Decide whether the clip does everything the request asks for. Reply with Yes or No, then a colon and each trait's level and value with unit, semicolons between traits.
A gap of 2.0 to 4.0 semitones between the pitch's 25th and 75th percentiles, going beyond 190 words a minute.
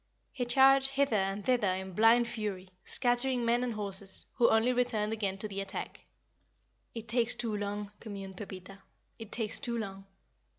No: average, 3.5 semitones; average, 165 wpm